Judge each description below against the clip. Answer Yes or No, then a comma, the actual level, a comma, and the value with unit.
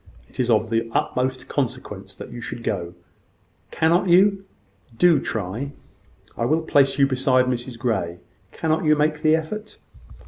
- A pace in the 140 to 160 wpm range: Yes, average, 150 wpm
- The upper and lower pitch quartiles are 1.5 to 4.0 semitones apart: No, average, 5.2 semitones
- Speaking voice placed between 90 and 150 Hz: Yes, low, 135 Hz